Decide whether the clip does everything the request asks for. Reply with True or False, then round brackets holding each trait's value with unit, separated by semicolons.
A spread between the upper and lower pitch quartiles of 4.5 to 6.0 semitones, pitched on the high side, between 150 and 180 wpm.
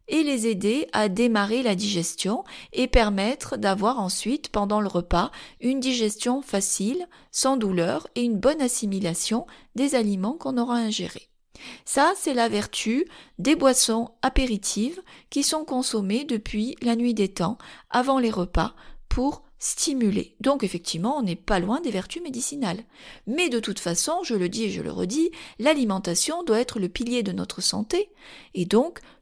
True (4.8 semitones; 235 Hz; 160 wpm)